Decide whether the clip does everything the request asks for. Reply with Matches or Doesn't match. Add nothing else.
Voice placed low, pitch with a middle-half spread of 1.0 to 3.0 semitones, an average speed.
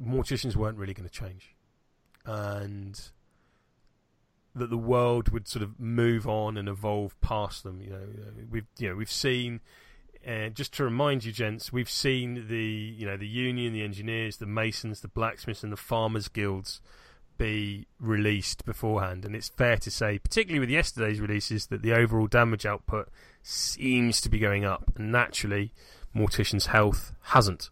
Matches